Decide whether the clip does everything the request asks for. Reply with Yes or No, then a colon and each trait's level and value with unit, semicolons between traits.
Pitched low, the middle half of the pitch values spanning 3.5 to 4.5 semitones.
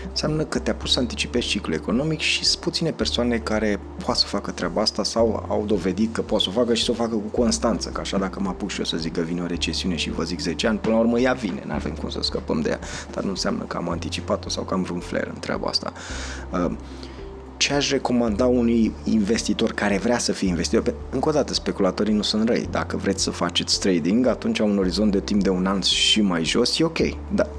No: low, 105 Hz; average, 5.2 semitones